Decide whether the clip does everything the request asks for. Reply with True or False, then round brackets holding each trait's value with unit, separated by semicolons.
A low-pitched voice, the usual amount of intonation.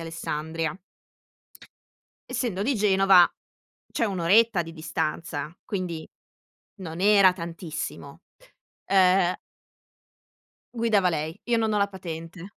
False (180 Hz; 3.5 semitones)